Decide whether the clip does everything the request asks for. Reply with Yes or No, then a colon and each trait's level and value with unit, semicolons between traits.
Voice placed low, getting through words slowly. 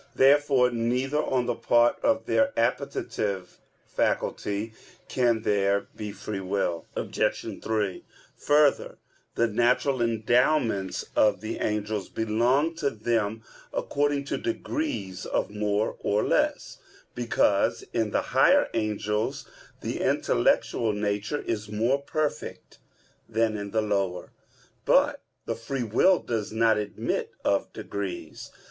Yes: low, 110 Hz; slow, 120 wpm